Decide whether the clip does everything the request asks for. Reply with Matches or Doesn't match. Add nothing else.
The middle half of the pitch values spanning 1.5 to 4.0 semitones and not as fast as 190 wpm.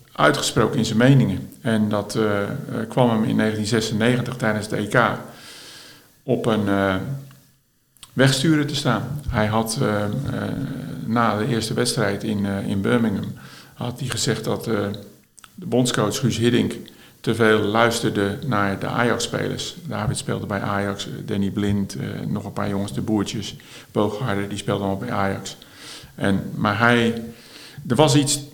Matches